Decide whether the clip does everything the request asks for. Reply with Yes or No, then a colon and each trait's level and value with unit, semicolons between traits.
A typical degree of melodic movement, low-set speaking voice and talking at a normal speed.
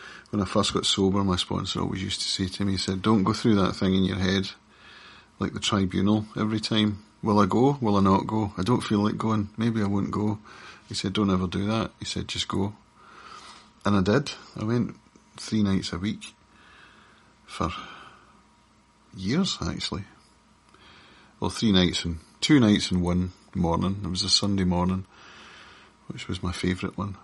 No: narrow, 2.2 semitones; low, 100 Hz; average, 185 wpm